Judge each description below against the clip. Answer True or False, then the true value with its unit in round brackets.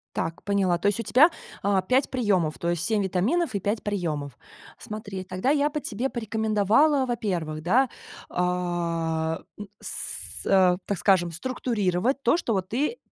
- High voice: True (200 Hz)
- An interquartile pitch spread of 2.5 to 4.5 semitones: False (5.1 semitones)